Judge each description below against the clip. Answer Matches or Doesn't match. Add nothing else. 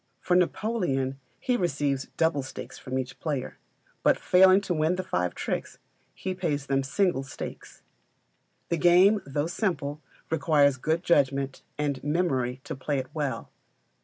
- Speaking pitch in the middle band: Matches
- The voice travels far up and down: Doesn't match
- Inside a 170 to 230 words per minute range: Doesn't match